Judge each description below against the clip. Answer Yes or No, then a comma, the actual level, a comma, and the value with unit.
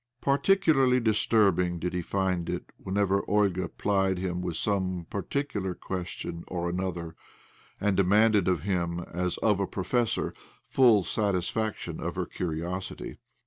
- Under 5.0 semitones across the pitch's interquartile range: Yes, average, 2.8 semitones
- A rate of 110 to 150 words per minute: Yes, slow, 135 wpm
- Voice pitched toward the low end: Yes, very low, 95 Hz